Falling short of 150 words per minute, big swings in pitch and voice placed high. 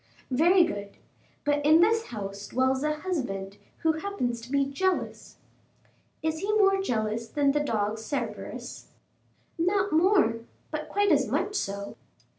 Yes: average, 140 wpm; wide, 8.5 semitones; very high, 290 Hz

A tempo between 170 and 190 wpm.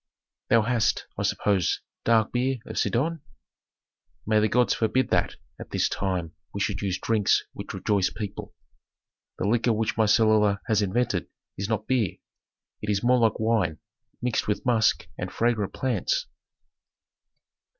No: average, 150 wpm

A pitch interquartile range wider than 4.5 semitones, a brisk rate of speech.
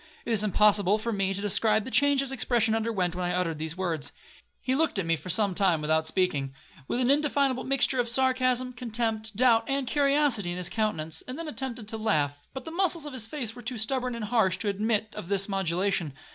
Yes: wide, 5.4 semitones; fast, 220 wpm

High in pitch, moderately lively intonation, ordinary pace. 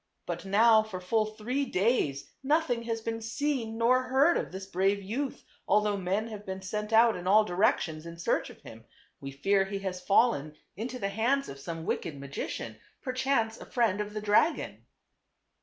Yes: high, 210 Hz; average, 3.8 semitones; average, 180 wpm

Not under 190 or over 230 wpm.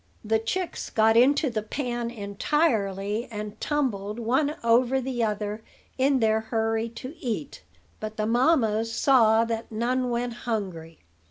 No: average, 140 wpm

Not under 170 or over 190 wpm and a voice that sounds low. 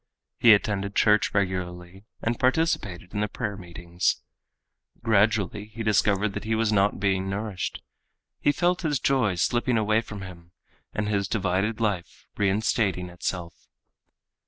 No: slow, 135 wpm; low, 105 Hz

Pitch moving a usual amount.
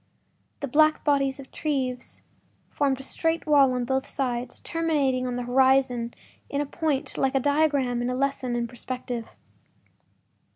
No: narrow, 2.3 semitones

